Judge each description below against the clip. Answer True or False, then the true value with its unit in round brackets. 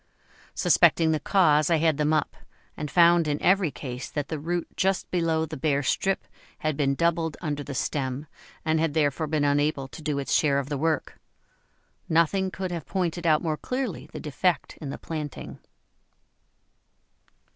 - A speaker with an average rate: True (170 wpm)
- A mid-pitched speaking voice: True (155 Hz)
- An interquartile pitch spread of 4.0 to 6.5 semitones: False (2.6 semitones)